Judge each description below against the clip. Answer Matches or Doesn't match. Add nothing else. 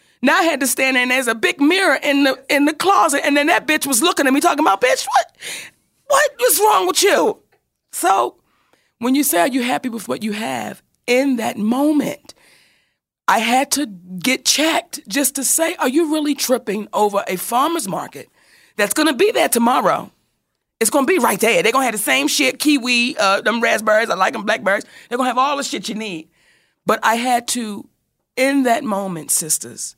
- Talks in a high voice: Matches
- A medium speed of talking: Doesn't match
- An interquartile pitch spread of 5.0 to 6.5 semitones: Matches